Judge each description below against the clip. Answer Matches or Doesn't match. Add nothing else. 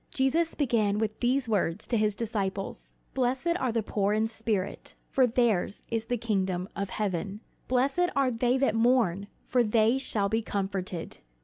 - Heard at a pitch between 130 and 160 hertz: Doesn't match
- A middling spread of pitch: Matches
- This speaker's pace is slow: Doesn't match